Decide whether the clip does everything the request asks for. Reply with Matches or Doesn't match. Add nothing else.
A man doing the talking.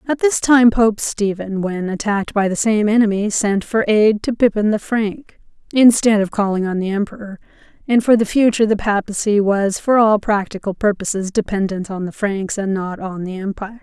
Doesn't match